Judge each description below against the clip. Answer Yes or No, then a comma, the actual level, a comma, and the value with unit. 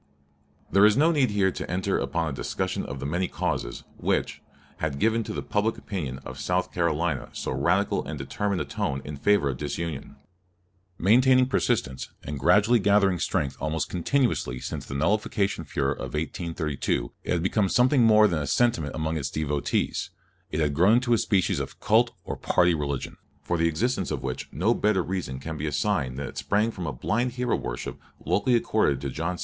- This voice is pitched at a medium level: No, very low, 90 Hz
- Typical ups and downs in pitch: No, wide, 6.4 semitones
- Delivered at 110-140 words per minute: No, average, 195 wpm